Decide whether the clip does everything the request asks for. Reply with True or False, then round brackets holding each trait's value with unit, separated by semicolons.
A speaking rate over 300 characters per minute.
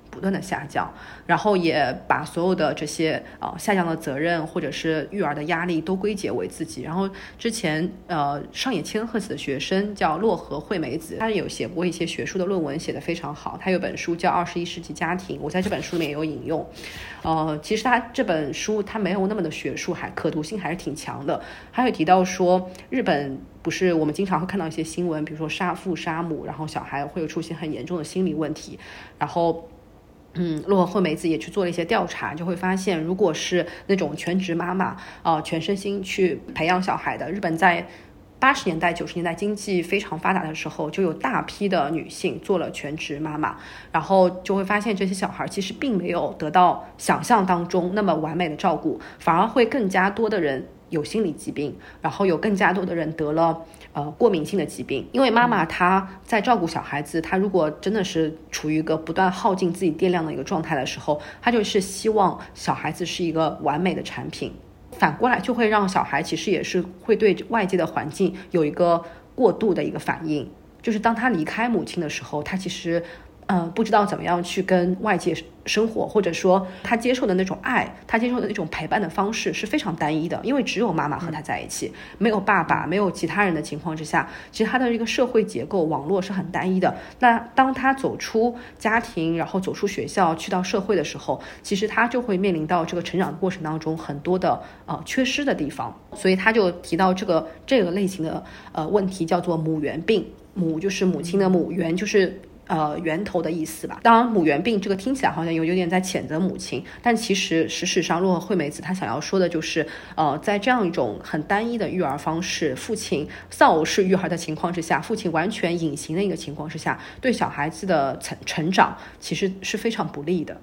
True (320 characters per minute)